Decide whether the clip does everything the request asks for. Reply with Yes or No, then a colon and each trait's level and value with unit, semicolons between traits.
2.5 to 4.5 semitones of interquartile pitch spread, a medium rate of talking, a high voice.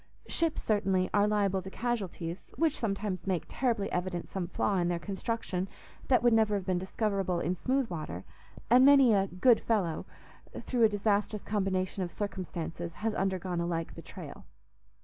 Yes: average, 3.4 semitones; average, 165 wpm; high, 195 Hz